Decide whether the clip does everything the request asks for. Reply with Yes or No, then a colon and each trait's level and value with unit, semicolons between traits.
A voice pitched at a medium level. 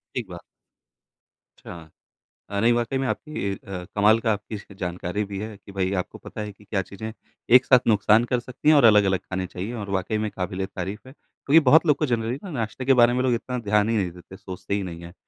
No: low, 105 Hz